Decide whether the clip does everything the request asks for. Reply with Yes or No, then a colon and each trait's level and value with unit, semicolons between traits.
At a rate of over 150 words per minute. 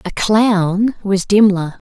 No: slow, 130 wpm